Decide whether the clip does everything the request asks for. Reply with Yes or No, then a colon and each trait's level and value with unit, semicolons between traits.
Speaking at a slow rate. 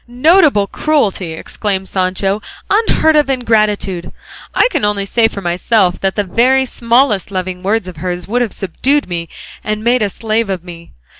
No: average, 165 wpm